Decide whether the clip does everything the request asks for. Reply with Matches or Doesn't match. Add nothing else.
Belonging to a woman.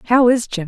Matches